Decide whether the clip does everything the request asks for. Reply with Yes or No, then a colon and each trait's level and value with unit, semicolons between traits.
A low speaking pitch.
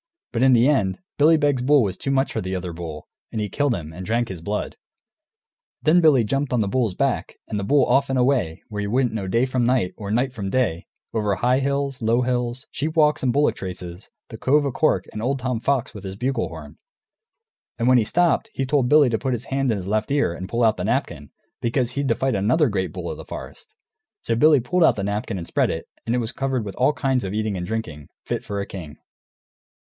Yes: low, 120 Hz